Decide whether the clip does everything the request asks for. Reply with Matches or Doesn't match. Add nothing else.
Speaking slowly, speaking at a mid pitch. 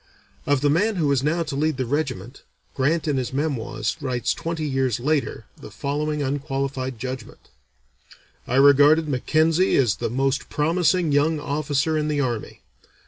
Doesn't match